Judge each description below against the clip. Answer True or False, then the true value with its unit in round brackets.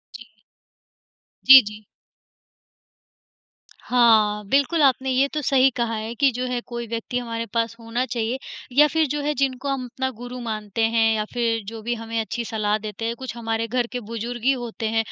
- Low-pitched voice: False (235 Hz)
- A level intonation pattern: True (2.2 semitones)